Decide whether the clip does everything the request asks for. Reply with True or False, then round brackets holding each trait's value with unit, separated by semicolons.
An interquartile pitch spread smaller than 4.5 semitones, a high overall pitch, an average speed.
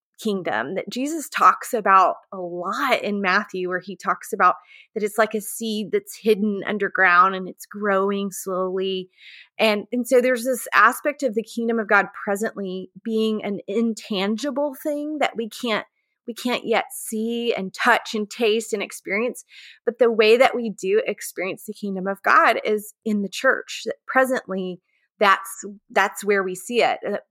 True (3.6 semitones; 215 Hz; 170 wpm)